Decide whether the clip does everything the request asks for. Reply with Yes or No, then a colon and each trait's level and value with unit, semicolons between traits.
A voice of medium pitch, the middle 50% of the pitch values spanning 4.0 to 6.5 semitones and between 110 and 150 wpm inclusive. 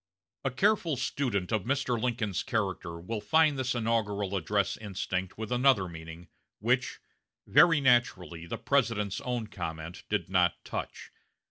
No: low, 105 Hz; average, 5.2 semitones; slow, 135 wpm